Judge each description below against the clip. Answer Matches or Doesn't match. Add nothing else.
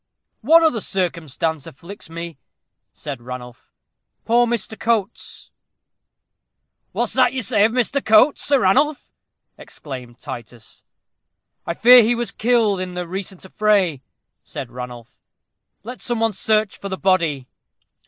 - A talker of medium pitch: Doesn't match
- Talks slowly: Matches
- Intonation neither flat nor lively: Doesn't match